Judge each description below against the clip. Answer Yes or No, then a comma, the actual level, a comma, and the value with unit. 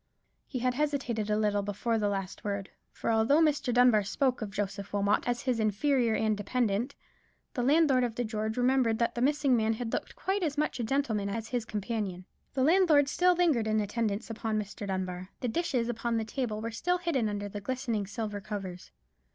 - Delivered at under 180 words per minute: No, average, 200 wpm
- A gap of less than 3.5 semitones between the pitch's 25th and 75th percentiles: No, average, 3.8 semitones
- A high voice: Yes, high, 225 Hz